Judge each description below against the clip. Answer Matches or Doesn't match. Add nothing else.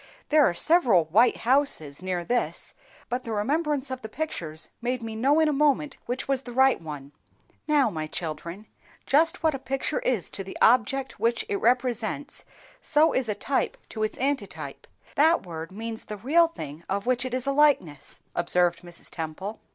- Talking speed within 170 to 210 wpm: Matches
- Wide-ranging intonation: Matches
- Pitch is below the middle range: Doesn't match